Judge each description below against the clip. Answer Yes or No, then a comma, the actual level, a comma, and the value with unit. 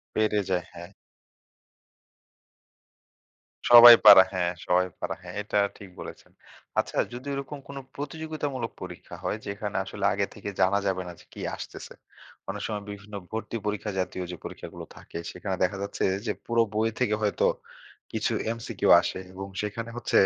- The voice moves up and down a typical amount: Yes, average, 3.4 semitones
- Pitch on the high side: No, low, 105 Hz